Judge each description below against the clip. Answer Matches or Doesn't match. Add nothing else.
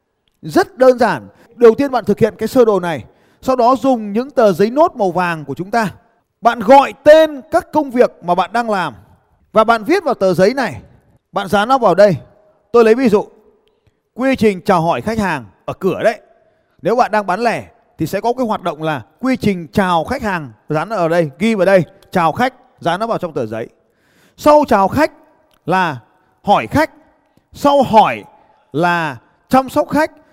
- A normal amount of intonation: Doesn't match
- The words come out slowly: Doesn't match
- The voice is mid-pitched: Doesn't match